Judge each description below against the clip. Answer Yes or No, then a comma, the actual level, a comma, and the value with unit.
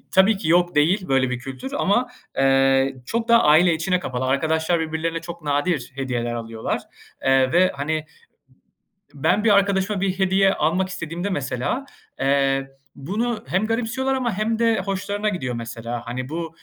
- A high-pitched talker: No, medium, 165 Hz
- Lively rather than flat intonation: Yes, wide, 6.6 semitones